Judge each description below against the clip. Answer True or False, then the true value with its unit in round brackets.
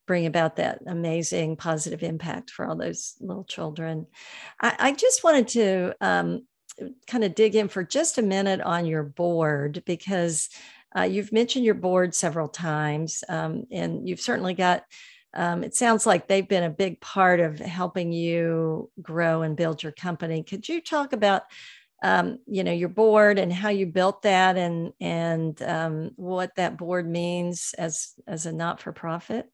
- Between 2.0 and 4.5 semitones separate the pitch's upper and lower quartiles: True (3.3 semitones)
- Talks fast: False (170 wpm)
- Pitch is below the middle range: False (180 Hz)